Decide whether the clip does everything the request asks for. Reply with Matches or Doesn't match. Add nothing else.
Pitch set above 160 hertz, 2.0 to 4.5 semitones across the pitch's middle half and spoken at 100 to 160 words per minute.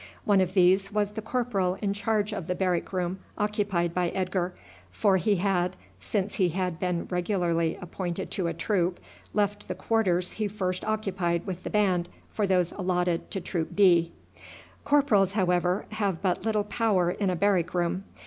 Doesn't match